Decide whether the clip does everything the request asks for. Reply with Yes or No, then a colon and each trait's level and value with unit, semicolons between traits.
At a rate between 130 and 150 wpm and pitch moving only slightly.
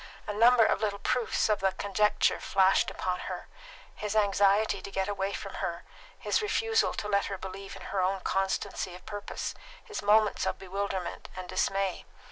No: average, 175 wpm; narrow, 1.7 semitones